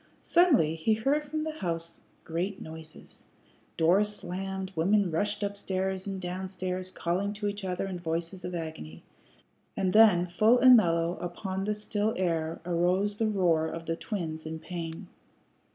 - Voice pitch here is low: No, medium, 185 Hz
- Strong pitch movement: No, average, 3.6 semitones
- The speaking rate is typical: Yes, average, 160 wpm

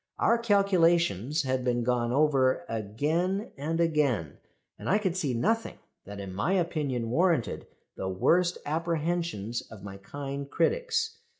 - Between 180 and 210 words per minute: No, slow, 135 wpm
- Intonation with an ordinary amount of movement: No, wide, 6.7 semitones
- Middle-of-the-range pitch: Yes, medium, 150 Hz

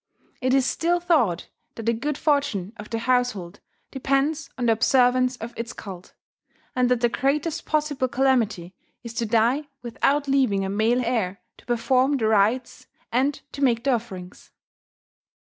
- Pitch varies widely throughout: No, average, 3.4 semitones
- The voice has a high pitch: Yes, high, 245 Hz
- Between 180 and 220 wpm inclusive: No, average, 160 wpm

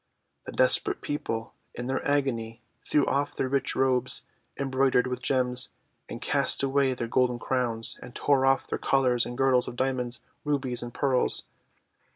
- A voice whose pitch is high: No, low, 130 Hz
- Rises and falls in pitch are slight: Yes, narrow, 1.8 semitones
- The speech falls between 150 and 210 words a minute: Yes, average, 160 wpm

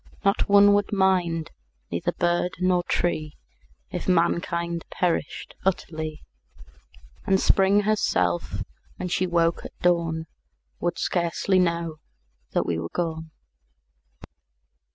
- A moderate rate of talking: No, slow, 110 wpm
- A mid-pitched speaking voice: Yes, medium, 175 Hz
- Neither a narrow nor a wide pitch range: No, narrow, 2.2 semitones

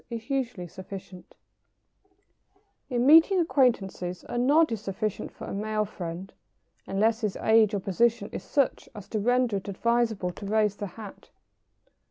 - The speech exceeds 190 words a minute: No, average, 140 wpm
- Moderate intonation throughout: Yes, average, 3.4 semitones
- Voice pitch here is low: No, high, 215 Hz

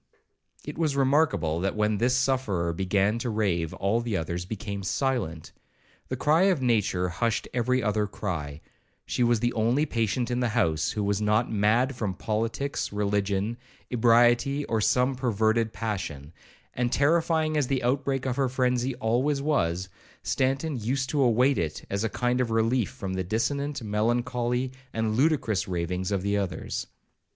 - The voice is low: Yes, low, 115 Hz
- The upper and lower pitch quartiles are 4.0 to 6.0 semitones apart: Yes, average, 4.4 semitones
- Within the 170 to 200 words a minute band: No, average, 160 wpm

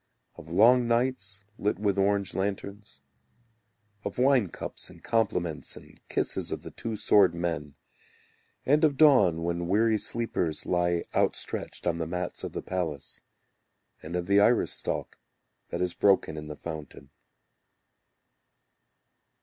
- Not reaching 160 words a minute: Yes, slow, 135 wpm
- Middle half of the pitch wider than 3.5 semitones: Yes, average, 4.4 semitones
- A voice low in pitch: Yes, very low, 95 Hz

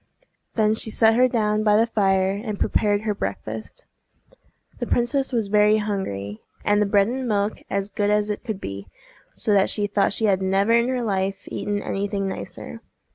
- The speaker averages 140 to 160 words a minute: No, average, 190 wpm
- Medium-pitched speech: No, high, 210 Hz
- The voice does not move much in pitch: Yes, narrow, 1.9 semitones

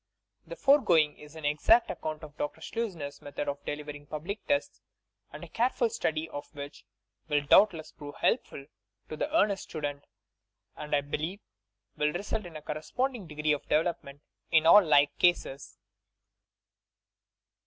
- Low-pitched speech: No, medium, 155 Hz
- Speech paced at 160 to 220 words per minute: No, average, 150 wpm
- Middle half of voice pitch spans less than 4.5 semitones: No, average, 4.8 semitones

